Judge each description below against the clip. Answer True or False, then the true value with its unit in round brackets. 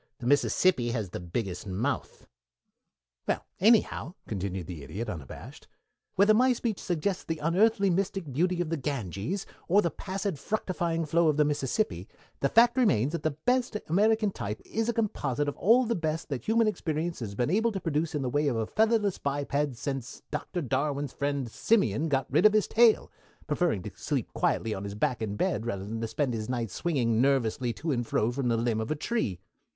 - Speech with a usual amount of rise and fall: False (8.5 semitones)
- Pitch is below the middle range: False (150 Hz)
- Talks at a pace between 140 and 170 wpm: False (195 wpm)